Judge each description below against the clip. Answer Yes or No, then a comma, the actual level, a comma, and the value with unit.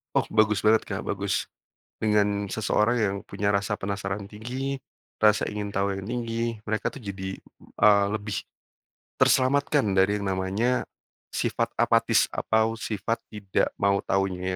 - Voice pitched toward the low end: Yes, low, 105 Hz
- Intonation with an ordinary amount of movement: No, narrow, 2.0 semitones